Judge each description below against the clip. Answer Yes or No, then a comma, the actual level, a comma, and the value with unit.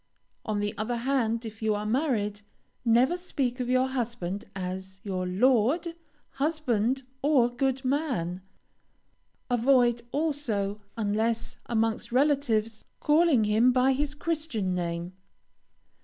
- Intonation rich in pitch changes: No, average, 4.3 semitones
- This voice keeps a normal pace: No, slow, 115 wpm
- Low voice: No, high, 235 Hz